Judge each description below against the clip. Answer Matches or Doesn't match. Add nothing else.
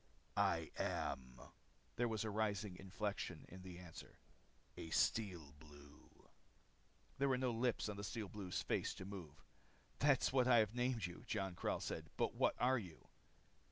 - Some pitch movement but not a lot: Matches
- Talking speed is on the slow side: Doesn't match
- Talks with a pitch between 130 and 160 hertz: Doesn't match